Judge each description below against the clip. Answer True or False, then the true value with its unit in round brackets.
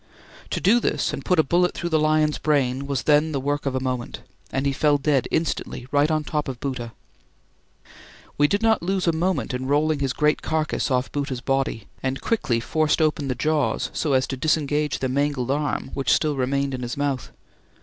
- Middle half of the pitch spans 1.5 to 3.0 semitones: True (2.7 semitones)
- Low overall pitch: False (145 Hz)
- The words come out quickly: True (210 wpm)